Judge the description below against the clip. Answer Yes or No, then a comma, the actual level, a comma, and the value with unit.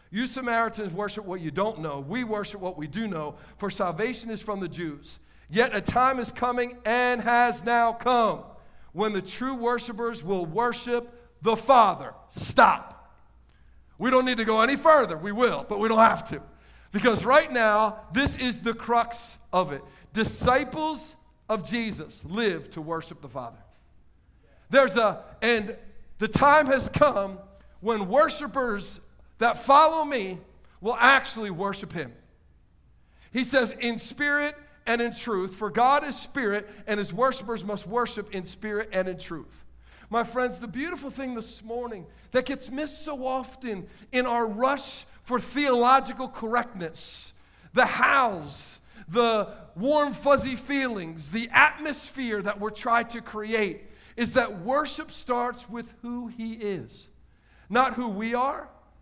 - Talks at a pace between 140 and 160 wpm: Yes, average, 150 wpm